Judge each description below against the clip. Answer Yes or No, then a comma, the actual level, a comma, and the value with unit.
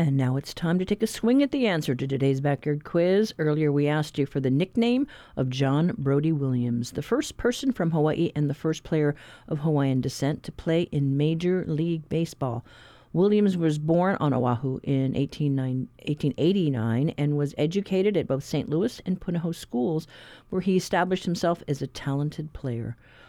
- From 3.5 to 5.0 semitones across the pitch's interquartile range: Yes, average, 4.1 semitones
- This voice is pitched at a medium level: Yes, medium, 150 Hz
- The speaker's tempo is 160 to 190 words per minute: Yes, average, 180 wpm